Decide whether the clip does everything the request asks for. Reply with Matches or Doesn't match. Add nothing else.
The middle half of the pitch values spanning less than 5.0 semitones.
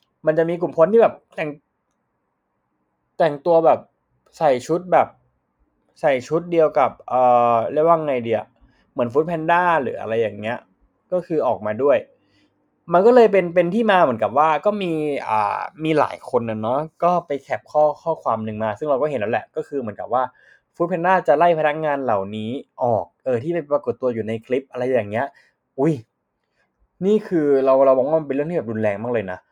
Doesn't match